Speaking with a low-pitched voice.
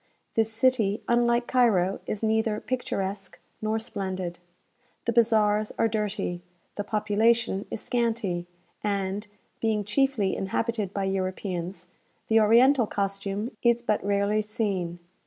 No: high, 210 Hz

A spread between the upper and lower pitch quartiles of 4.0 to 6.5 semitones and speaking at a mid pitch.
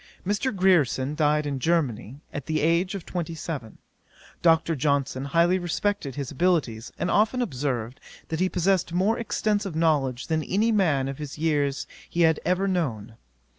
Yes: average, 4.7 semitones; medium, 160 Hz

